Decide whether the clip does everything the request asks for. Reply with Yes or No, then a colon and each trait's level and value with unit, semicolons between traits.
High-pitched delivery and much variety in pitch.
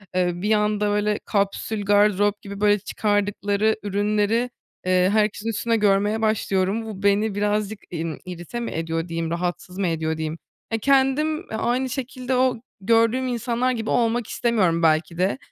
No: high, 210 Hz; average, 3.3 semitones